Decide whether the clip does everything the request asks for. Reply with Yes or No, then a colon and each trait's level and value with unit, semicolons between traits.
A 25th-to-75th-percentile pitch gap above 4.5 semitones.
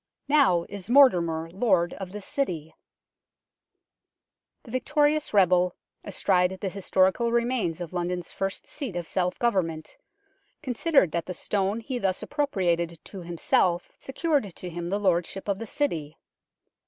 Yes: wide, 5.4 semitones